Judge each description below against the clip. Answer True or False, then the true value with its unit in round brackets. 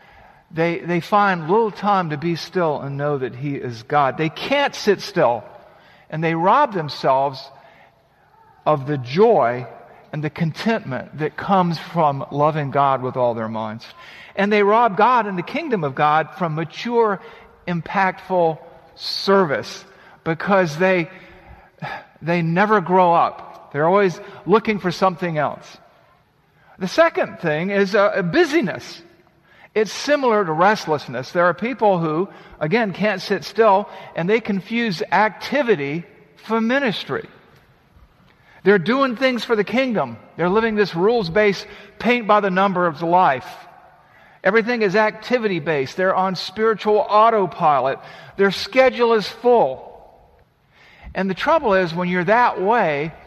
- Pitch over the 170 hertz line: True (190 Hz)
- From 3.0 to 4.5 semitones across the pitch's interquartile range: False (4.9 semitones)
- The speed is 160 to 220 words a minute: False (135 wpm)